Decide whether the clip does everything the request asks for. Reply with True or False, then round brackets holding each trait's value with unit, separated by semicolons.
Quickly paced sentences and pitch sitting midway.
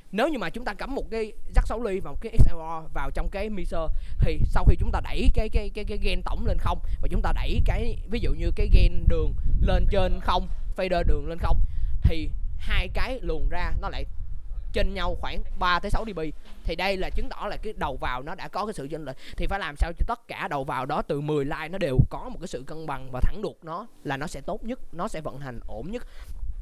True (265 wpm; 150 Hz)